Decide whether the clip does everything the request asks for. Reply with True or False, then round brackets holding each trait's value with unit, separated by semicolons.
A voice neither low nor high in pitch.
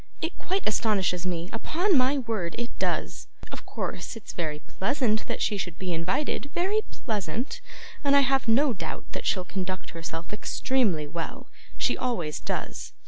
False (215 Hz)